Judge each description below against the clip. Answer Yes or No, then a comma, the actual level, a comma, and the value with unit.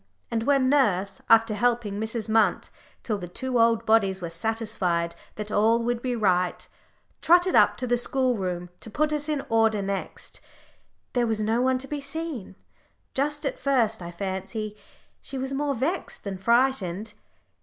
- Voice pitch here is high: Yes, high, 225 Hz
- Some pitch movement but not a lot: Yes, average, 4.6 semitones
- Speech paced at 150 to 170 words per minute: Yes, average, 165 wpm